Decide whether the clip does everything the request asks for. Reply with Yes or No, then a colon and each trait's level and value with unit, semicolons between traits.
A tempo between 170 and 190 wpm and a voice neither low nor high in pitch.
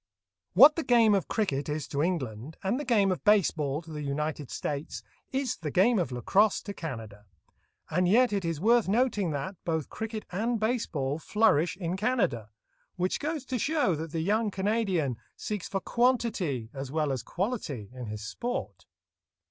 Yes: average, 180 wpm; medium, 180 Hz